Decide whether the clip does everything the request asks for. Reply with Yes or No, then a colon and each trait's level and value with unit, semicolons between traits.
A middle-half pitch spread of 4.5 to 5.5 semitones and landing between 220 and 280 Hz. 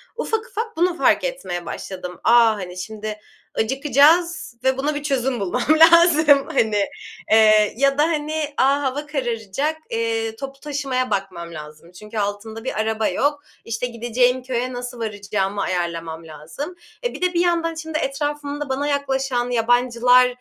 Yes: average, 5.2 semitones; very high, 250 Hz